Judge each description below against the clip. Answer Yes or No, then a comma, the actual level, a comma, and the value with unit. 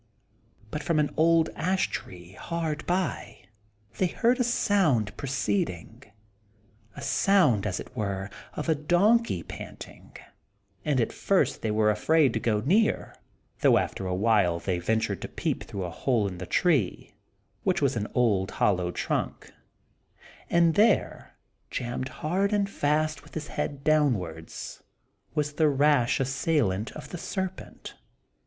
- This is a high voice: No, medium, 140 Hz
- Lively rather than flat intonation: Yes, wide, 8.0 semitones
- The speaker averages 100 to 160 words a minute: Yes, average, 145 wpm